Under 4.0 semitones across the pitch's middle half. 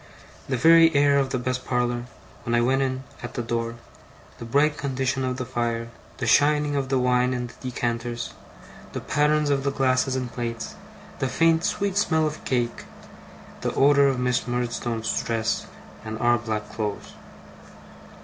Yes: average, 2.9 semitones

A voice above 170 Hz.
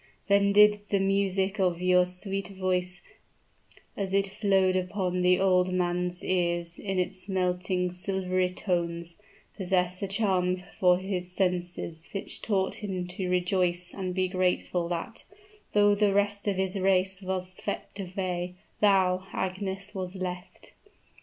Yes: medium, 185 Hz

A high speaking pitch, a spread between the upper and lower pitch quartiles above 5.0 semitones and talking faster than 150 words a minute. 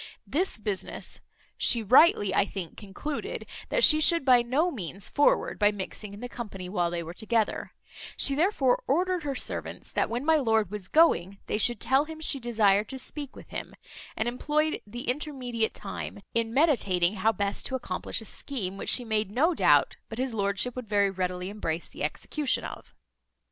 Yes: high, 230 Hz; wide, 5.6 semitones; average, 185 wpm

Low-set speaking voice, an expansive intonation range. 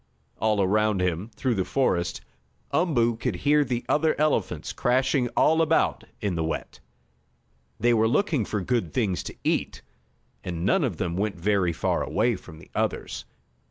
Yes: low, 110 Hz; wide, 6.2 semitones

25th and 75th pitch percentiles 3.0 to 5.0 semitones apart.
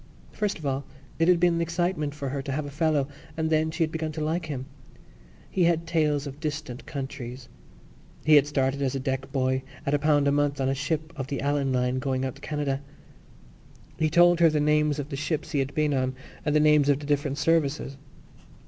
No: narrow, 2.5 semitones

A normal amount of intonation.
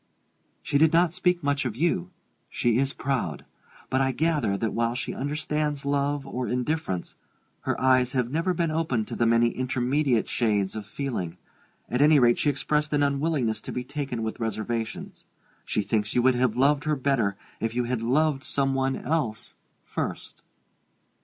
Yes: average, 3.9 semitones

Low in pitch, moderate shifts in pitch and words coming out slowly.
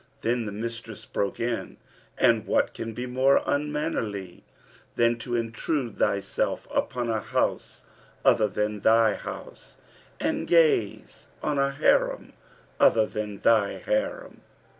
Yes: low, 115 Hz; average, 4.0 semitones; slow, 125 wpm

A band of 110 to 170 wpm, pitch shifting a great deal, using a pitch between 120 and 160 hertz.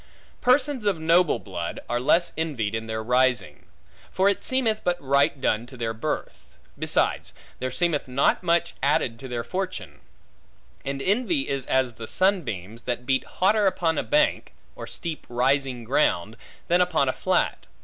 Yes: average, 160 wpm; wide, 6.8 semitones; medium, 140 Hz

